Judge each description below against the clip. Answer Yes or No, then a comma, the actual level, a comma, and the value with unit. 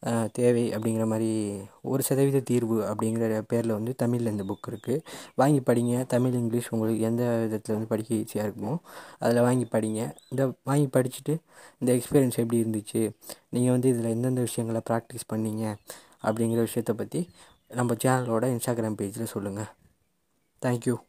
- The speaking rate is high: Yes, fast, 140 wpm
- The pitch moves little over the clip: Yes, narrow, 2.1 semitones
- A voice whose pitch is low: Yes, low, 115 Hz